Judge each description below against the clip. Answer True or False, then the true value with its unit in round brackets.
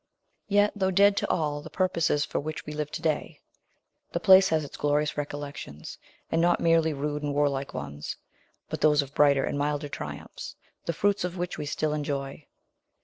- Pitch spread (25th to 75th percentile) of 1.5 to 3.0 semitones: True (2.7 semitones)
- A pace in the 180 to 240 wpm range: True (185 wpm)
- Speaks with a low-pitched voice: False (150 Hz)